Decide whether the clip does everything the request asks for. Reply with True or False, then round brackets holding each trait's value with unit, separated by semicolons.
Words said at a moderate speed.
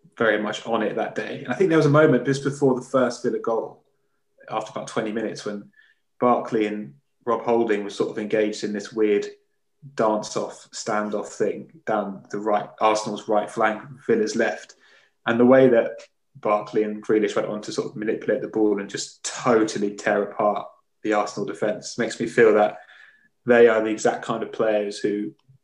True (190 wpm)